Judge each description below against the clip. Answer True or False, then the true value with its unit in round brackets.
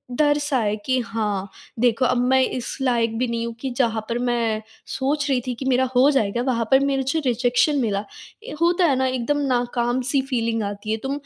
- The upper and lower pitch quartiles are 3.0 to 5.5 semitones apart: False (2.6 semitones)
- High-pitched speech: True (250 Hz)